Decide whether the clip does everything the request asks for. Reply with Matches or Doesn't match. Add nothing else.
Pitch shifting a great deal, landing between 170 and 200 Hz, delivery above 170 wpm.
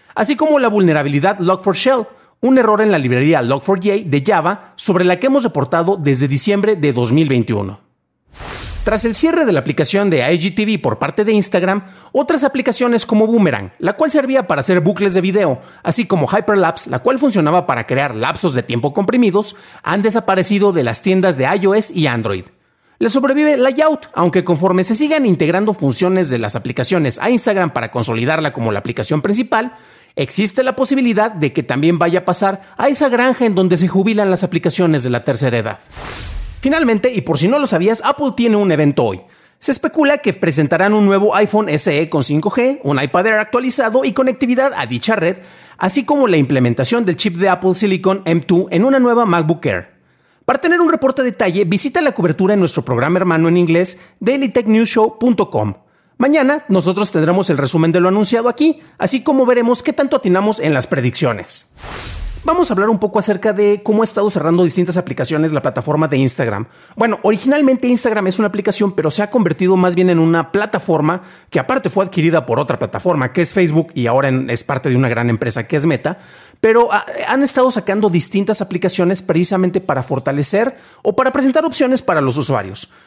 Matches